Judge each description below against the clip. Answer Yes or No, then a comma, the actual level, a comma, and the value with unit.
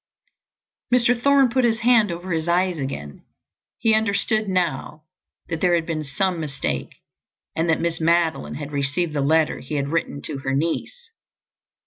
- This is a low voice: No, medium, 170 Hz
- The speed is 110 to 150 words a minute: No, average, 160 wpm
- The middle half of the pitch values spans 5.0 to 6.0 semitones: Yes, wide, 5.6 semitones